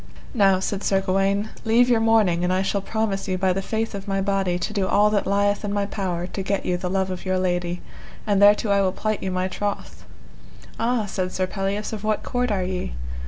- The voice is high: Yes, high, 195 Hz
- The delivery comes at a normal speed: No, fast, 230 wpm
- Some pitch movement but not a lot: No, narrow, 2.0 semitones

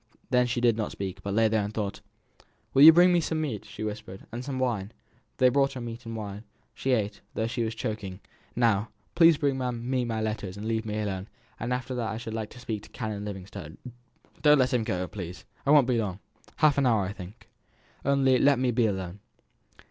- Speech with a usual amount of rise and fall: Yes, average, 3.7 semitones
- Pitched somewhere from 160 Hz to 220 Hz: No, low, 115 Hz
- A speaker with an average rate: No, fast, 215 wpm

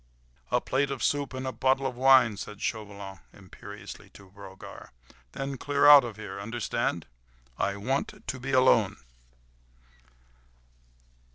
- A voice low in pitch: Yes, low, 120 Hz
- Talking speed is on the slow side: Yes, slow, 125 wpm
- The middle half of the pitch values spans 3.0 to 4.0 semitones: No, average, 4.9 semitones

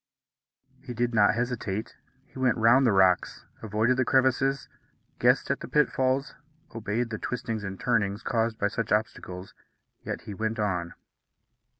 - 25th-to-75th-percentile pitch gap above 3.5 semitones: No, average, 3.2 semitones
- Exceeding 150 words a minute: No, average, 145 wpm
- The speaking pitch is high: No, low, 115 Hz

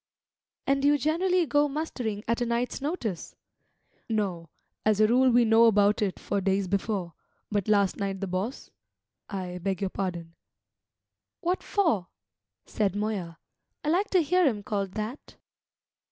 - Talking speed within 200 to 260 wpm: No, average, 155 wpm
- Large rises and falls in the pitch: Yes, wide, 6.0 semitones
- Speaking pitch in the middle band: No, high, 215 Hz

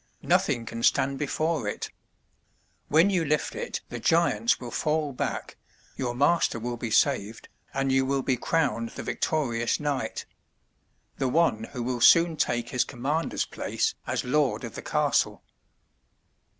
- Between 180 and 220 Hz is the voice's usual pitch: No, low, 135 Hz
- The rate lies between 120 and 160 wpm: Yes, average, 150 wpm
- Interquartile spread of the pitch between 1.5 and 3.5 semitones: No, average, 4.4 semitones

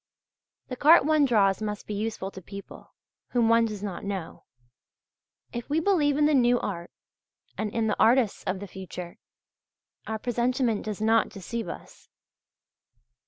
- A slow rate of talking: No, average, 155 wpm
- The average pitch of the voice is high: Yes, high, 220 Hz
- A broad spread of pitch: No, average, 3.7 semitones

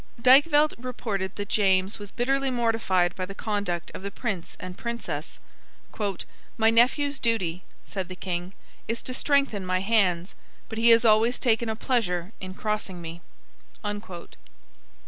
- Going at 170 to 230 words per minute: No, average, 145 wpm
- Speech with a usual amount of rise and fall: Yes, average, 4.2 semitones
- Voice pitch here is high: Yes, high, 215 Hz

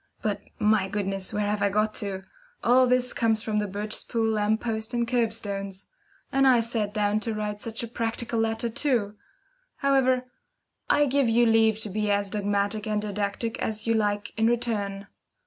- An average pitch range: No, narrow, 2.1 semitones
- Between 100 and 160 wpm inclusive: No, average, 180 wpm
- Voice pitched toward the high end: Yes, high, 220 Hz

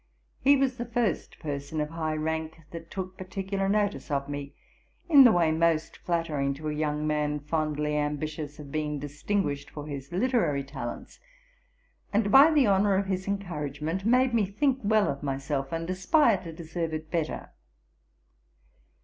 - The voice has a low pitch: No, medium, 160 Hz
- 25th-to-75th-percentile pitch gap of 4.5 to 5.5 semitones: Yes, average, 5.1 semitones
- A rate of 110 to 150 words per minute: No, average, 160 wpm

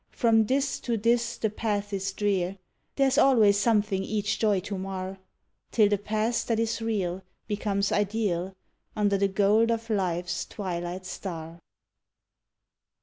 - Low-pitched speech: No, high, 205 Hz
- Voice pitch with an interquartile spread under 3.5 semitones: Yes, average, 2.7 semitones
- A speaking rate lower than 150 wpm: Yes, average, 140 wpm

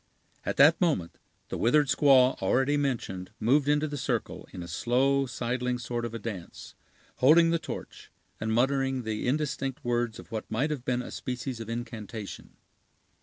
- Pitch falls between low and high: No, low, 125 Hz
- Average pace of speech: Yes, average, 170 wpm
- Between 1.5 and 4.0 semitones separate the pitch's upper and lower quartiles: Yes, average, 3.3 semitones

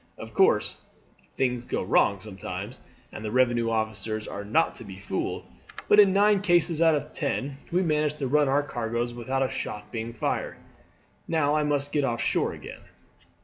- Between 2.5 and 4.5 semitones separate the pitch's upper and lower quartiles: No, average, 5.2 semitones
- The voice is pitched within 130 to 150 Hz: Yes, low, 135 Hz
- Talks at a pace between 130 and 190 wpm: Yes, average, 180 wpm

